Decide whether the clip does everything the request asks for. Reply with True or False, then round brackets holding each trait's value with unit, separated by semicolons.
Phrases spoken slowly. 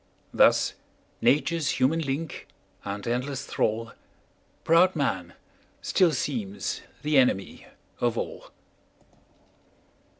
True (90 wpm)